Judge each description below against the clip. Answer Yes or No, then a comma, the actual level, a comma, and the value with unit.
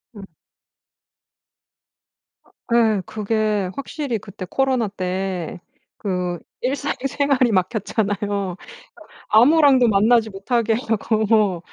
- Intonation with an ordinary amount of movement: Yes, average, 3.9 semitones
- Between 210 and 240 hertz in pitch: Yes, high, 215 Hz